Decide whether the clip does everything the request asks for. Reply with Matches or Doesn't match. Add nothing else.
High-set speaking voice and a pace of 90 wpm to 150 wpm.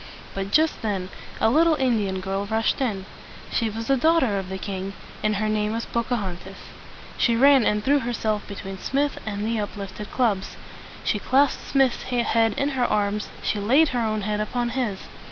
Doesn't match